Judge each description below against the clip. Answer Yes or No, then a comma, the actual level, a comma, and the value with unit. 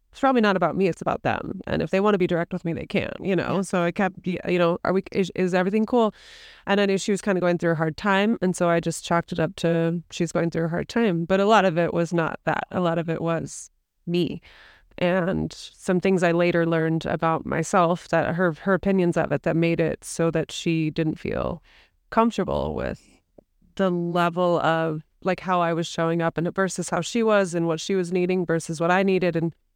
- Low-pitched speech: No, medium, 175 Hz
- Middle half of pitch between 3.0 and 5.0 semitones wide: No, narrow, 2.4 semitones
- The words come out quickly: Yes, fast, 245 wpm